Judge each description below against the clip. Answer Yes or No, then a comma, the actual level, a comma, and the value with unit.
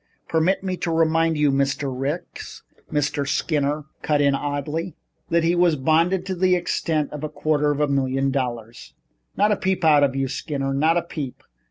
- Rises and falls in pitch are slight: No, average, 3.2 semitones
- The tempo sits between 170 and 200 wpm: Yes, average, 185 wpm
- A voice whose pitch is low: No, medium, 150 Hz